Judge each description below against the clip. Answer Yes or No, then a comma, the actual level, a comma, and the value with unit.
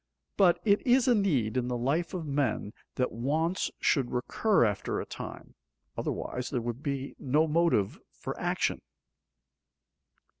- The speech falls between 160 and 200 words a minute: No, average, 145 wpm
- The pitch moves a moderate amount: No, wide, 5.9 semitones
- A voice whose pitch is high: No, medium, 140 Hz